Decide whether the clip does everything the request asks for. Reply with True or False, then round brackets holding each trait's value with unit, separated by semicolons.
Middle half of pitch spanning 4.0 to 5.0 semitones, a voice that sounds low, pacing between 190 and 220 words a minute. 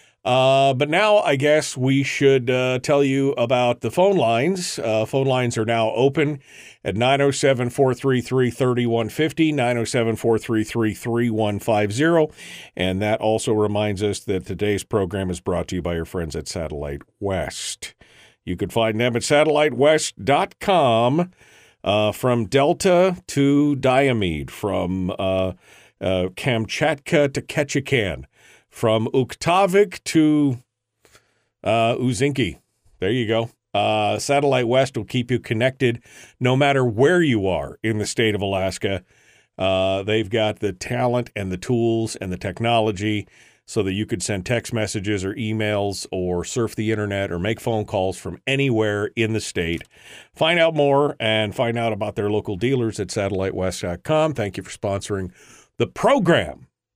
False (4.7 semitones; 115 Hz; 145 wpm)